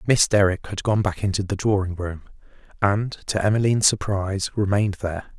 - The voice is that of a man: Yes, male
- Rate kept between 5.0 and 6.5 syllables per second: Yes, 5.8 syllables/s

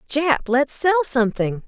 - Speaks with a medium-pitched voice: No, very high, 250 Hz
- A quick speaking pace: No, average, 145 wpm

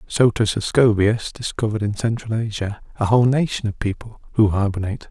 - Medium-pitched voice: No, low, 110 Hz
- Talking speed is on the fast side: No, average, 155 wpm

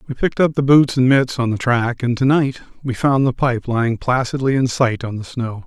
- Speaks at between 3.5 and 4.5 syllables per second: No, 5.3 syllables/s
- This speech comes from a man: Yes, male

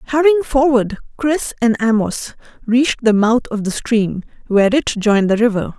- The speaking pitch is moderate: No, high, 235 Hz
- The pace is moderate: Yes, average, 165 wpm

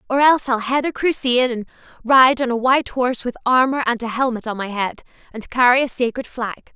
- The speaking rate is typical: No, fast, 220 wpm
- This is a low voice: No, very high, 250 Hz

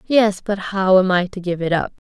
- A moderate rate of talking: No, fast, 260 wpm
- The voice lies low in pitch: No, high, 190 Hz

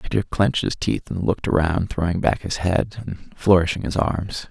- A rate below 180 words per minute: No, average, 200 wpm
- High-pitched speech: No, very low, 95 Hz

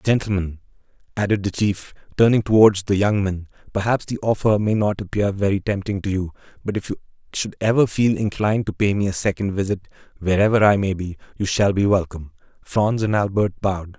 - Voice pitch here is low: Yes, low, 100 Hz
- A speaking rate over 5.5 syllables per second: Yes, 5.7 syllables/s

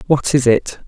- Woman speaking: Yes, female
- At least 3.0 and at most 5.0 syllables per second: Yes, 4.3 syllables/s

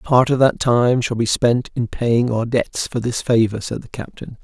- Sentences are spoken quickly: Yes, fast, 230 wpm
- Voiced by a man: Yes, male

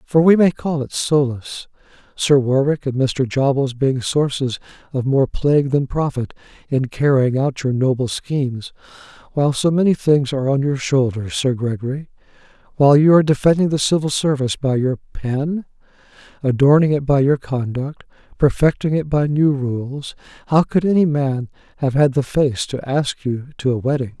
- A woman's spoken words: No, male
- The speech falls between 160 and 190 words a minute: Yes, average, 165 wpm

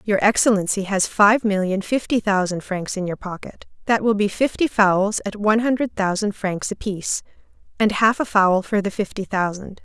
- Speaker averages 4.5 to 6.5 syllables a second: Yes, 5.0 syllables/s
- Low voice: No, high, 205 Hz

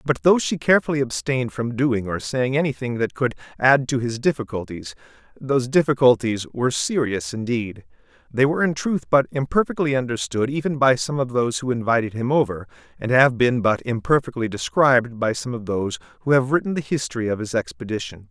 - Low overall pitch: Yes, low, 125 Hz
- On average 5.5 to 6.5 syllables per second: Yes, 5.8 syllables/s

